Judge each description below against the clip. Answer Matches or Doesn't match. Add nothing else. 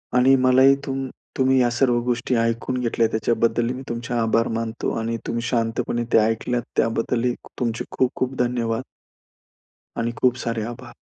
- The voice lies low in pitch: Matches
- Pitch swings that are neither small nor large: Doesn't match